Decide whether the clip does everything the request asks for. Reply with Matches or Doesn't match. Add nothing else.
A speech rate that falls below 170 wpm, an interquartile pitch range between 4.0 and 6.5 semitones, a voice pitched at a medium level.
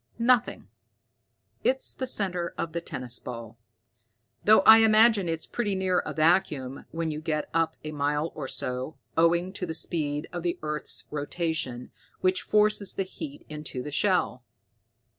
Matches